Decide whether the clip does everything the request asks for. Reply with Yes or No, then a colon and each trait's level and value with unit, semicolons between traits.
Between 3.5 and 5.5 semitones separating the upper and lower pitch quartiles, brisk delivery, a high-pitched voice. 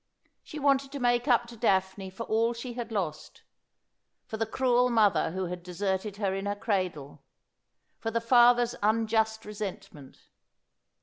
No: average, 3.8 semitones; average, 150 wpm; high, 220 Hz